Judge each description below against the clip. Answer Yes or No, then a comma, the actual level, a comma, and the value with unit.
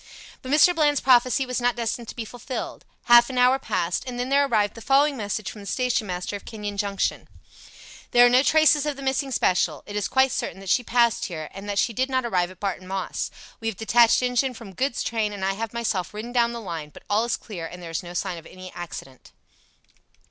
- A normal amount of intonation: Yes, average, 4.6 semitones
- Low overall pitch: No, high, 230 Hz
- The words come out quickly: Yes, fast, 235 wpm